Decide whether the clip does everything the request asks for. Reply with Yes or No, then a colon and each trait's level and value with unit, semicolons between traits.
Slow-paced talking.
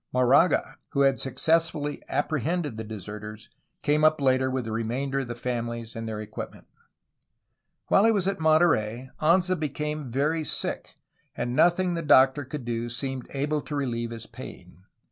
No: average, 165 wpm